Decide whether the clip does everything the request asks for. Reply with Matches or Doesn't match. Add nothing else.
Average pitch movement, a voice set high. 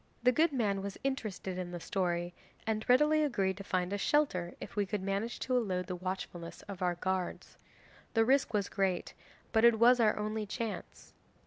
Matches